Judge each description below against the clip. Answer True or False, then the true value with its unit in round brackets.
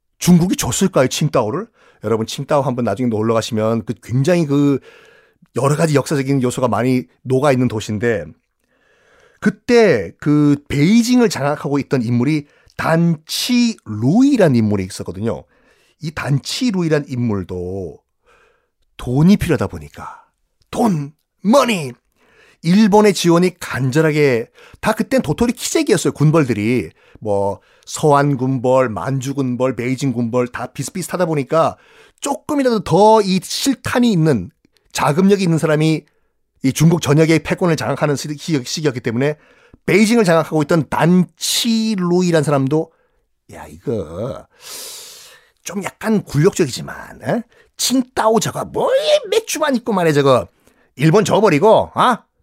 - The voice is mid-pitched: True (155 Hz)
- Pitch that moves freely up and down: True (7.5 semitones)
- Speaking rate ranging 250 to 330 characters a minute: True (285 characters per minute)